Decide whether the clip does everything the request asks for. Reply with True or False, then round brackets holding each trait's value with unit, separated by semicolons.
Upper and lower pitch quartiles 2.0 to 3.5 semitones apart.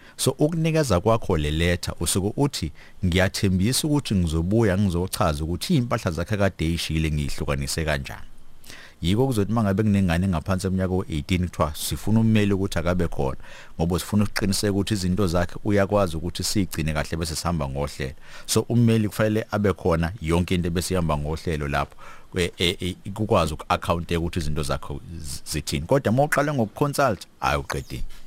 False (4.5 semitones)